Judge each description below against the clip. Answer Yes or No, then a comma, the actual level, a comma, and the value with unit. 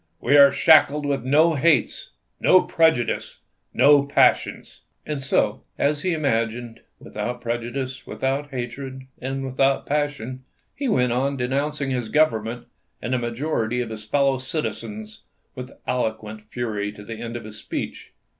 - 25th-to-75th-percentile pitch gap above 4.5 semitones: No, average, 3.4 semitones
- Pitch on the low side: Yes, low, 130 Hz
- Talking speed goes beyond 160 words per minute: No, average, 150 wpm